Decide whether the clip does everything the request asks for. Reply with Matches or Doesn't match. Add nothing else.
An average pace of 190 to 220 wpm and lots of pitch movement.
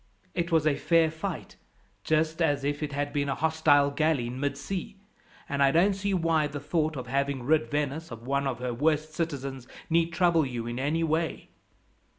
Doesn't match